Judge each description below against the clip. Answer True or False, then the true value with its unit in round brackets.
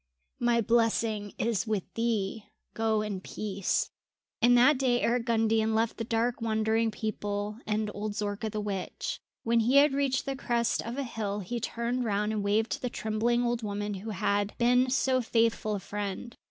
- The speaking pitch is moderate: False (225 Hz)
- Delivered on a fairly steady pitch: True (2.2 semitones)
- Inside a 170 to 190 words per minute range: True (180 wpm)